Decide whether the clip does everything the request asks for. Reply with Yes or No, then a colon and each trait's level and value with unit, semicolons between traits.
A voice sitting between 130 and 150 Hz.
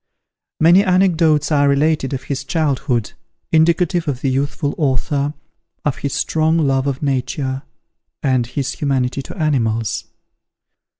Yes: medium, 140 Hz